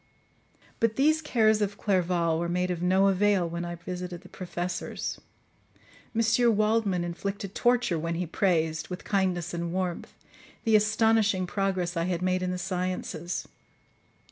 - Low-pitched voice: No, medium, 185 Hz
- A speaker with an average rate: Yes, average, 145 wpm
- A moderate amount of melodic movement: Yes, average, 3.0 semitones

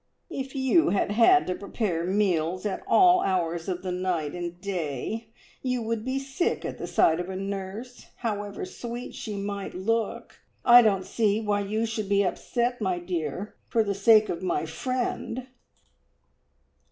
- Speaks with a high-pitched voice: Yes, high, 205 Hz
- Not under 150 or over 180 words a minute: Yes, average, 165 wpm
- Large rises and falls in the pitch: No, average, 4.1 semitones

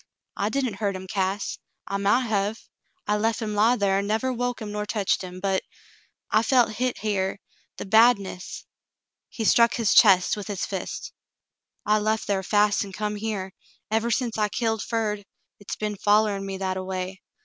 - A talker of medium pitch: No, high, 210 Hz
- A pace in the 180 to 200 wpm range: Yes, average, 190 wpm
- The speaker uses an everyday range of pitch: No, narrow, 2.1 semitones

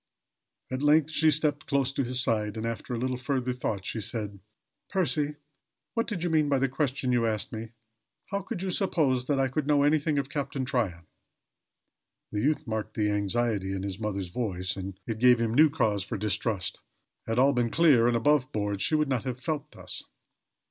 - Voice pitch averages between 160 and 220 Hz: No, low, 125 Hz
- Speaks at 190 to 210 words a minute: Yes, average, 200 wpm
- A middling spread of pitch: Yes, average, 5.0 semitones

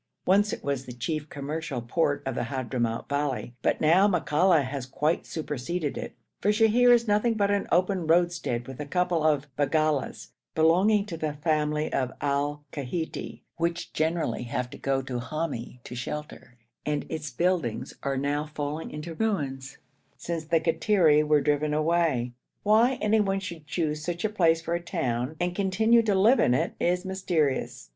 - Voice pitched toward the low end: No, medium, 155 Hz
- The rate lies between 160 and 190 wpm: Yes, average, 170 wpm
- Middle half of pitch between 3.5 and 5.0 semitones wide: Yes, average, 4.2 semitones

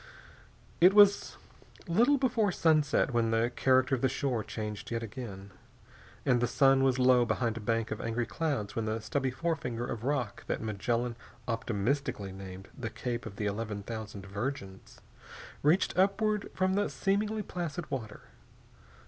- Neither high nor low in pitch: No, low, 120 Hz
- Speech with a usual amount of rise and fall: No, wide, 5.8 semitones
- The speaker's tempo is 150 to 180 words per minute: Yes, average, 155 wpm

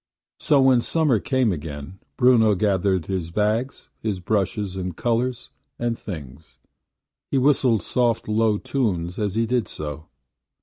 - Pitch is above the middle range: No, low, 105 Hz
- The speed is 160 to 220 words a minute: No, slow, 135 wpm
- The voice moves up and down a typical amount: Yes, average, 4.9 semitones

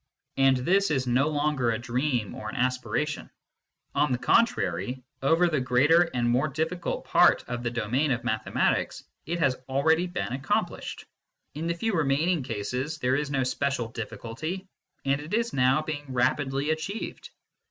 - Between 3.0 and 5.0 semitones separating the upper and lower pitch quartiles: Yes, average, 3.8 semitones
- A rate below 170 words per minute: Yes, average, 160 wpm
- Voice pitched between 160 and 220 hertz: No, medium, 140 Hz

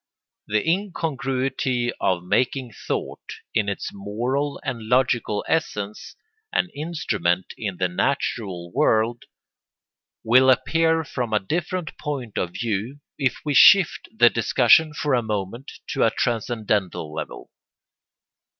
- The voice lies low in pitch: Yes, low, 120 Hz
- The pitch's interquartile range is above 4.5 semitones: Yes, average, 5.2 semitones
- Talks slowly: Yes, slow, 125 wpm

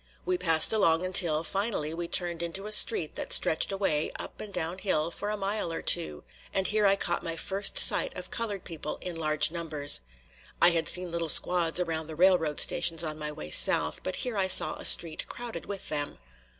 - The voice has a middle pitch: Yes, medium, 170 Hz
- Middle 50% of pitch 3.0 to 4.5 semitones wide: Yes, average, 3.5 semitones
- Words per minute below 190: No, fast, 205 wpm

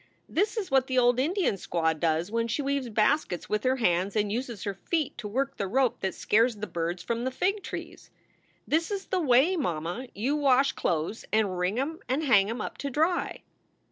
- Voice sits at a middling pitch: No, high, 245 Hz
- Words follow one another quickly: Yes, fast, 210 wpm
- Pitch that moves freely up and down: Yes, wide, 5.8 semitones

